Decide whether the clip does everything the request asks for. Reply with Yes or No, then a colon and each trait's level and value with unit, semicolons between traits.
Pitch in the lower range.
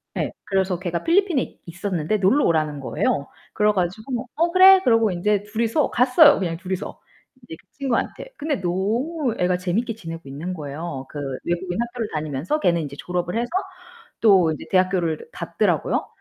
No: high, 190 Hz